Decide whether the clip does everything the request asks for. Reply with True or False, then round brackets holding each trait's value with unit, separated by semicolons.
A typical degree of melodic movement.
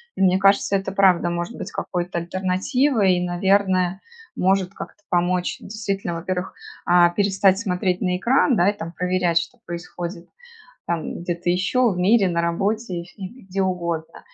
False (2.0 semitones)